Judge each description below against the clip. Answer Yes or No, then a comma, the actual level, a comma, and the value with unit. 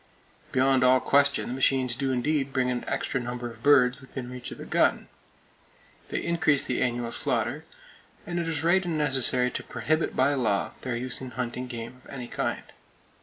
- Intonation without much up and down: Yes, narrow, 2.3 semitones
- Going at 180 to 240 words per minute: Yes, average, 185 wpm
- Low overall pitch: Yes, low, 130 Hz